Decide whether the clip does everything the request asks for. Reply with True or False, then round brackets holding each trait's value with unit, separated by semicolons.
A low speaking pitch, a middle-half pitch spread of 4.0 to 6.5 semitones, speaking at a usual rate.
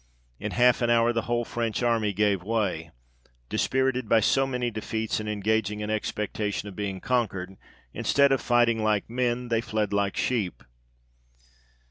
False (110 Hz; 2.5 semitones; 155 wpm)